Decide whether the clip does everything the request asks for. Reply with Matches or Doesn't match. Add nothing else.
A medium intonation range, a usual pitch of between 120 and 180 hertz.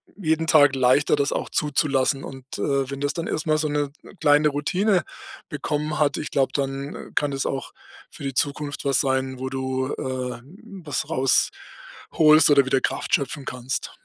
Doesn't match